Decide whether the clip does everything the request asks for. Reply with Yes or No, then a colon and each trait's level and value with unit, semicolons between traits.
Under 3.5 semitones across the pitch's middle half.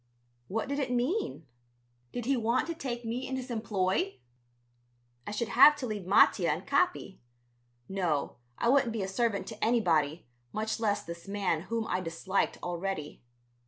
No: average, 4.6 semitones